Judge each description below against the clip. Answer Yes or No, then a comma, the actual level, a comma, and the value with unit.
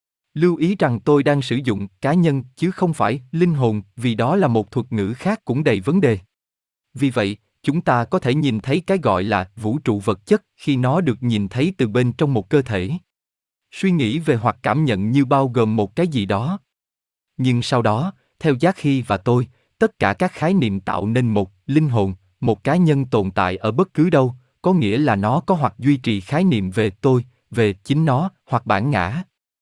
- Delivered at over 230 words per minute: No, average, 220 wpm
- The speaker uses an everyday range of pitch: No, wide, 6.4 semitones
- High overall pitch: No, low, 125 Hz